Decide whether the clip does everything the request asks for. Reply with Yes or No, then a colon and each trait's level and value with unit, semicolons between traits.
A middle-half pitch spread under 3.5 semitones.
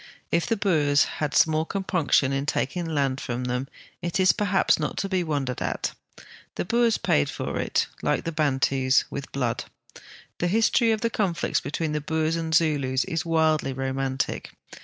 No: average, 4.6 semitones